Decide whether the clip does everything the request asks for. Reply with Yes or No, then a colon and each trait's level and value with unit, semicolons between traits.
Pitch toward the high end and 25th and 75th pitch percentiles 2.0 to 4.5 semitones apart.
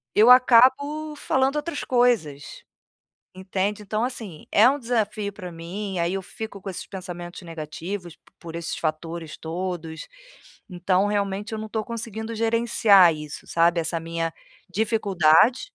No: high, 195 Hz; average, 5.0 semitones